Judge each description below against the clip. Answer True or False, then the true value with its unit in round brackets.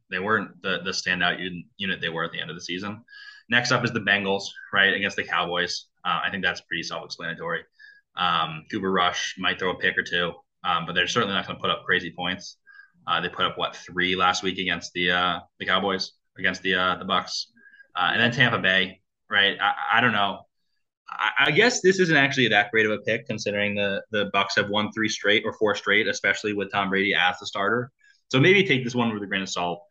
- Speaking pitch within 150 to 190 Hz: False (105 Hz)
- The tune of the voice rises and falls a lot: True (7.0 semitones)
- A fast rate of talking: True (235 wpm)